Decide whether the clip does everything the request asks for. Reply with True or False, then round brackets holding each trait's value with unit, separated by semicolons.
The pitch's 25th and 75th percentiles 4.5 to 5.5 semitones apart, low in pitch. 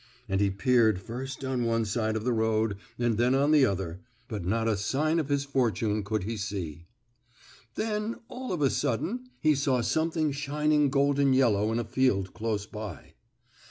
True (5.0 semitones; 120 Hz)